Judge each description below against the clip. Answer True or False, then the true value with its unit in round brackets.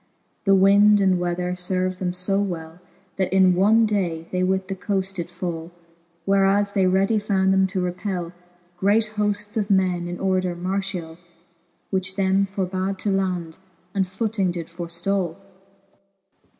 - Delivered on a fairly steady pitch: True (1.7 semitones)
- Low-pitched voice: False (190 Hz)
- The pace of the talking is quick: False (150 wpm)